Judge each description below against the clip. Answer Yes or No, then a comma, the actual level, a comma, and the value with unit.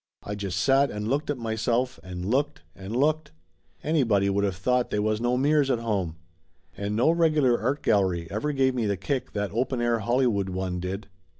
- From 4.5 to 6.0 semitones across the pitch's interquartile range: Yes, average, 5.0 semitones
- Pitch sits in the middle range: No, low, 115 Hz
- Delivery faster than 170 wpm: Yes, average, 195 wpm